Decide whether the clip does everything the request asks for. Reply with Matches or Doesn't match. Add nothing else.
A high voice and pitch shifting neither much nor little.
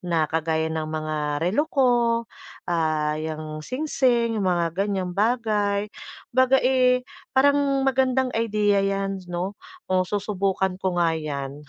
Doesn't match